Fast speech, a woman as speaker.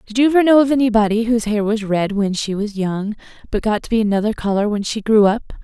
Yes: fast, 255 wpm; female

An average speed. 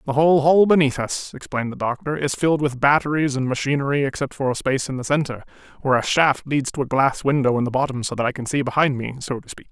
No: fast, 260 wpm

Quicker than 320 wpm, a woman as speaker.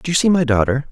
No: fast, 330 wpm; male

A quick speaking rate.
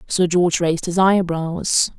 No: average, 150 wpm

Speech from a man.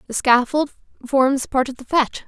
No: female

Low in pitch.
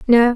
No: high, 240 Hz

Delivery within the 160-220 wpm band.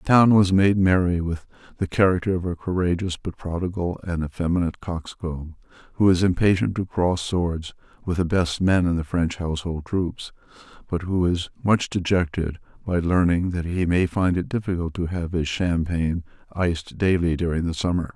Yes: average, 175 wpm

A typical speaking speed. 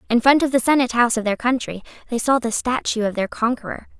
No: fast, 240 wpm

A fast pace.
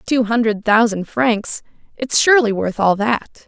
No: average, 140 wpm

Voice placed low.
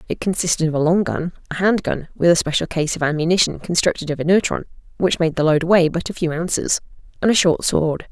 No: medium, 170 Hz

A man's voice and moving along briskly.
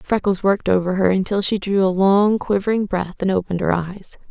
No: female; fast, 210 wpm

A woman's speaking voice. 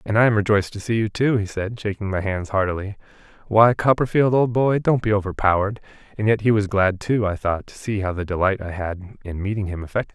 No: male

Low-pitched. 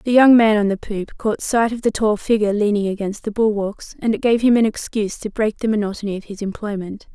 No: high, 215 Hz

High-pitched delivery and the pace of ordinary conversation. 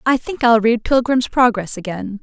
Yes: high, 230 Hz; average, 190 wpm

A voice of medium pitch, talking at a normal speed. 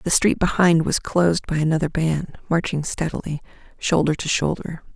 Yes: medium, 165 Hz; average, 160 wpm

